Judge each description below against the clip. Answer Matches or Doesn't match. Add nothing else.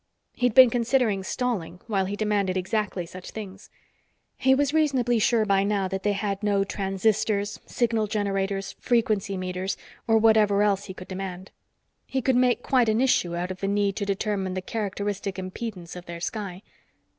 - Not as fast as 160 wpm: Doesn't match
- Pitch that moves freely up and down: Doesn't match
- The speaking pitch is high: Matches